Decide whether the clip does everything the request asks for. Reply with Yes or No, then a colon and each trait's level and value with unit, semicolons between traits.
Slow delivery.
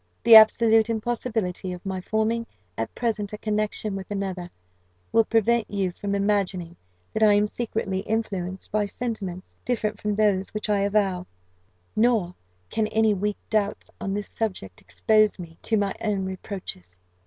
No: average, 155 wpm